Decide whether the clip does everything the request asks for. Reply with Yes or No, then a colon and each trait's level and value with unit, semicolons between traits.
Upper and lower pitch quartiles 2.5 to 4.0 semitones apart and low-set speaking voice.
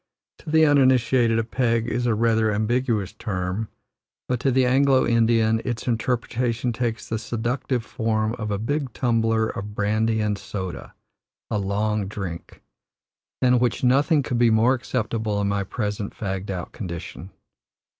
Yes: average, 2.8 semitones; low, 115 Hz